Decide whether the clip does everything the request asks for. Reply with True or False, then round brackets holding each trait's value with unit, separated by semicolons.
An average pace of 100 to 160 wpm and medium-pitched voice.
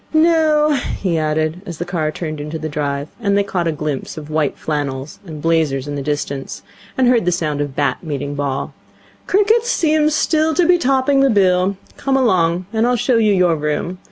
False (200 wpm; 175 Hz)